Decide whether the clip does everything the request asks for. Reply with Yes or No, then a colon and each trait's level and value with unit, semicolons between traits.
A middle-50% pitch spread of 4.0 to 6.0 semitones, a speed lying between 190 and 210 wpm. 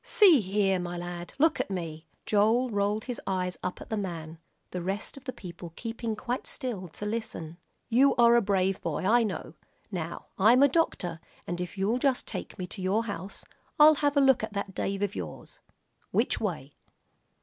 Yes: average, 4.8 semitones; average, 195 wpm